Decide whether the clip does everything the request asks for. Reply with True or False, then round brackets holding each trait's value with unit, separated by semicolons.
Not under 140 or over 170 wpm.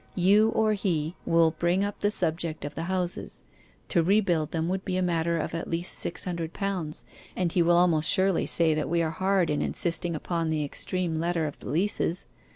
False (205 wpm)